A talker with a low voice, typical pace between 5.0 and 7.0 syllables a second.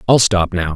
Yes: very low, 95 Hz; 5.1 syllables/s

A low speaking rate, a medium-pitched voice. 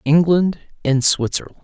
Yes: slow, 110 wpm; medium, 155 Hz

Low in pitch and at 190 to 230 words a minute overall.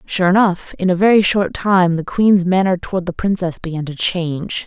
No: medium, 180 Hz; fast, 205 wpm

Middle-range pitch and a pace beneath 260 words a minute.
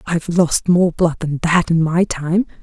Yes: medium, 170 Hz; fast, 205 wpm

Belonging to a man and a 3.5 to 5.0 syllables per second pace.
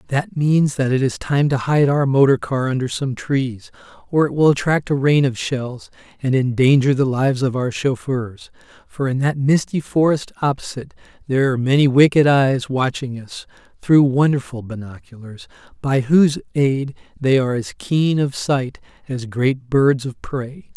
Yes: male; 4.7 syllables/s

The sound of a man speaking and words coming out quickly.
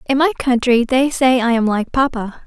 No: female; fast, 220 wpm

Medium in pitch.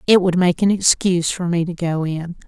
Yes: medium, 175 Hz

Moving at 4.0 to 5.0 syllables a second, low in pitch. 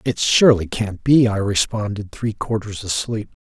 Yes: 4.7 syllables/s; low, 105 Hz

